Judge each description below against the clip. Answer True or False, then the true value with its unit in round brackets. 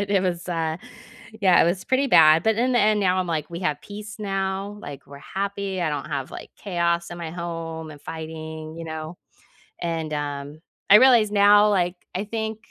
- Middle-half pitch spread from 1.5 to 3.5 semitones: False (4.3 semitones)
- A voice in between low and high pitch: True (175 Hz)